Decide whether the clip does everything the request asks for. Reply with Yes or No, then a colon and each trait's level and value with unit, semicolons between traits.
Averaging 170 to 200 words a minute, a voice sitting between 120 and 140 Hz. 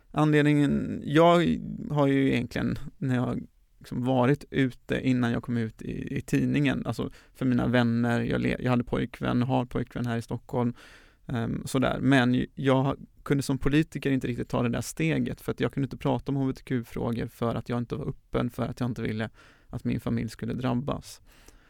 Yes: average, 190 wpm; low, 125 Hz